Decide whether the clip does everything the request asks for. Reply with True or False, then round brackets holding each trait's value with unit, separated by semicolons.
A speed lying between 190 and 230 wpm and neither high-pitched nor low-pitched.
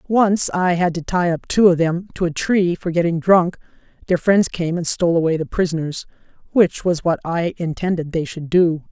True (200 wpm; 175 Hz)